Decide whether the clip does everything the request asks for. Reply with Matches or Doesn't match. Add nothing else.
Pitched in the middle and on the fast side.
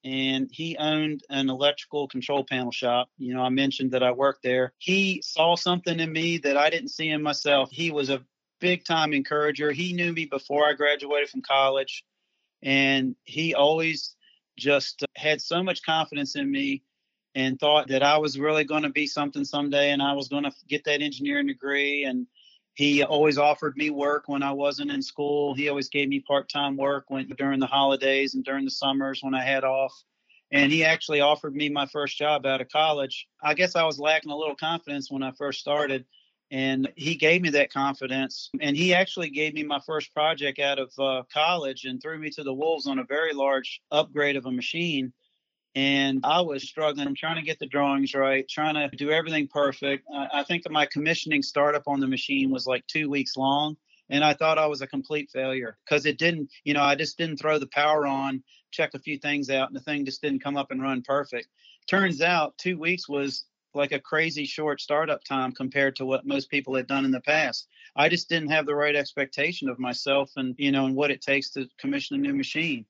Matches